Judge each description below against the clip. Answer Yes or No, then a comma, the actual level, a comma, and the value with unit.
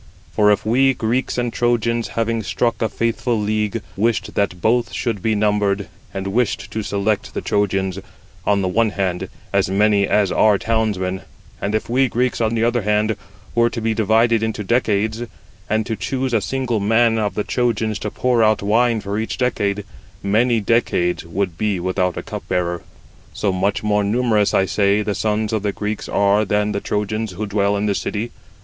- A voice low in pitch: Yes, low, 105 Hz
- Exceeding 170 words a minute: Yes, average, 190 wpm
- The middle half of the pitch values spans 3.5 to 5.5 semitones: No, narrow, 2.4 semitones